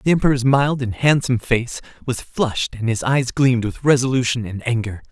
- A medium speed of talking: Yes, average, 190 wpm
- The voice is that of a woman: No, male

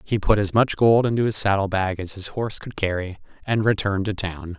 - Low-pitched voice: Yes, low, 100 Hz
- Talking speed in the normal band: No, fast, 235 wpm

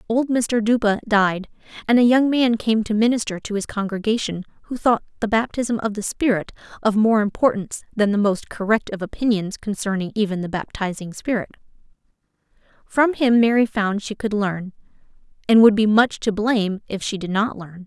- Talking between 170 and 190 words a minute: Yes, average, 180 wpm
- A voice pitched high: Yes, high, 215 Hz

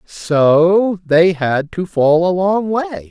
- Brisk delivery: No, average, 155 wpm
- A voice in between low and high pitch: Yes, medium, 175 Hz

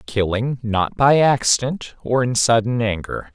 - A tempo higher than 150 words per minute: No, average, 145 wpm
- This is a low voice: Yes, low, 120 Hz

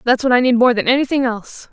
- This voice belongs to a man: No, female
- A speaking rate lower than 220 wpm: No, fast, 280 wpm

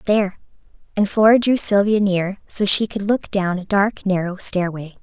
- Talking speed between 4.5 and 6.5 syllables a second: Yes, 4.8 syllables/s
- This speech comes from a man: No, female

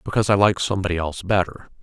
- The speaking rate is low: No, average, 200 wpm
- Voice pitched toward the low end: Yes, very low, 95 Hz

